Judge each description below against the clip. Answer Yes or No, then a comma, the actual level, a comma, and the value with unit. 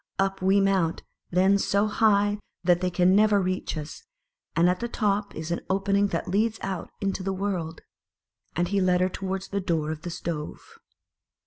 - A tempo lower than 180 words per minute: No, average, 185 wpm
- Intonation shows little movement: Yes, narrow, 2.2 semitones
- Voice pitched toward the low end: No, high, 190 Hz